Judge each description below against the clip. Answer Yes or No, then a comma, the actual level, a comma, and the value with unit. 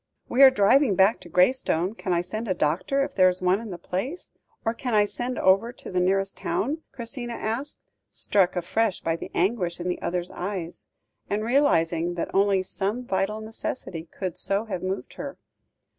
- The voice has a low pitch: No, high, 195 Hz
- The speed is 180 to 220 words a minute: Yes, average, 190 wpm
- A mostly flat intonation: No, average, 4.4 semitones